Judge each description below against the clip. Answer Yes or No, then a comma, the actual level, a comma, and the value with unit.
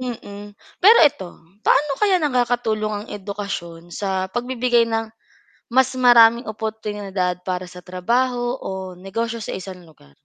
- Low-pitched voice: No, high, 220 Hz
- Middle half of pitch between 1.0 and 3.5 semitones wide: No, average, 4.5 semitones